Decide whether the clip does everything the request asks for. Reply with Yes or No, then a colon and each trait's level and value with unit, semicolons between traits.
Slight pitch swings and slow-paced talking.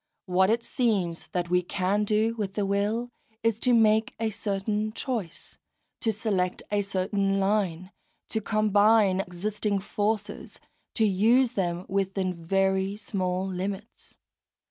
Yes: narrow, 2.3 semitones; slow, 130 wpm